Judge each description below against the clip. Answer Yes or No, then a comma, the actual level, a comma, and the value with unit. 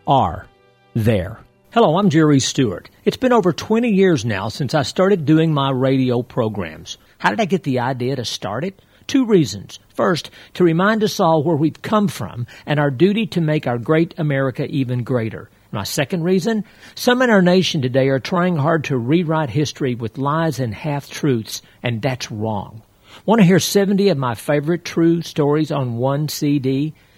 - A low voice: No, medium, 150 Hz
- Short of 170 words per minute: No, average, 185 wpm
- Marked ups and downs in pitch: Yes, wide, 6.0 semitones